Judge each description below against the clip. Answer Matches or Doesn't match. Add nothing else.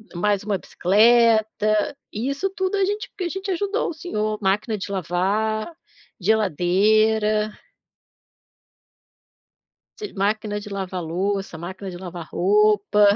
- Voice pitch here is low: Doesn't match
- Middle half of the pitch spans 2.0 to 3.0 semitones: Matches